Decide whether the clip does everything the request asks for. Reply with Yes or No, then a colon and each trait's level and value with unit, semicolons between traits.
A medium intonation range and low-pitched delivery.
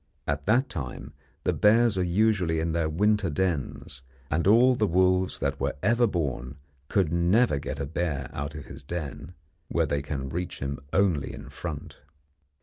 No: wide, 5.7 semitones; very low, 85 Hz